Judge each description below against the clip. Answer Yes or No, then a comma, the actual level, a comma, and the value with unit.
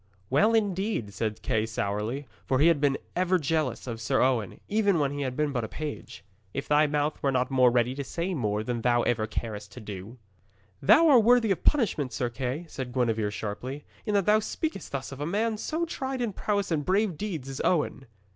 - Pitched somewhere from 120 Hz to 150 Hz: Yes, medium, 140 Hz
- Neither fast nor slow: No, fast, 215 wpm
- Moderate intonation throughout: No, wide, 8.0 semitones